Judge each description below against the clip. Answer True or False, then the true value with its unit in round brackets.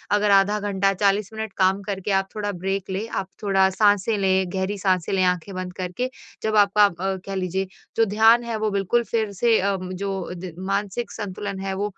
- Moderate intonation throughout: False (1.7 semitones)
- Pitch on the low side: False (195 Hz)